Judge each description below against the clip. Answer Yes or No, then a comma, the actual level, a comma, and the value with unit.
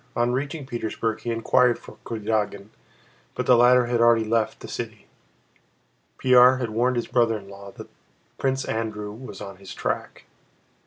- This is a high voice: No, low, 115 Hz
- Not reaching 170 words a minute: Yes, average, 160 wpm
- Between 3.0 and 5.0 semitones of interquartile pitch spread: No, narrow, 2.5 semitones